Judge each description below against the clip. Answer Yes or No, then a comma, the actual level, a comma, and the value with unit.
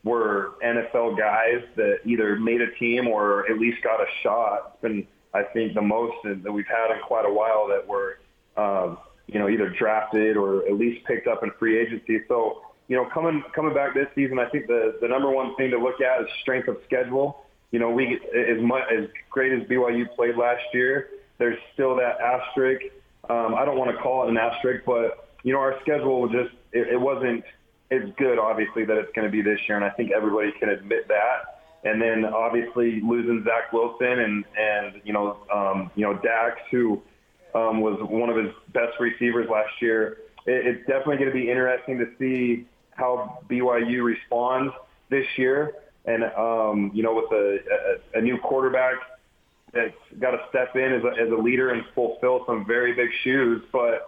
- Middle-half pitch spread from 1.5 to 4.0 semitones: Yes, narrow, 2.5 semitones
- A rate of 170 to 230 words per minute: Yes, average, 200 wpm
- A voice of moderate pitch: No, low, 120 Hz